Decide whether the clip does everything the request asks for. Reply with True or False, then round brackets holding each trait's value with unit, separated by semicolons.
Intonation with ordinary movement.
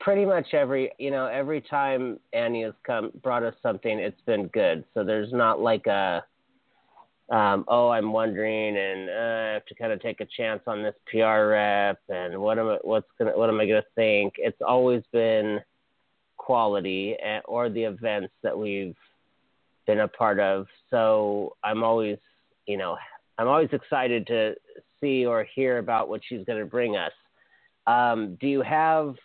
True (3.7 semitones)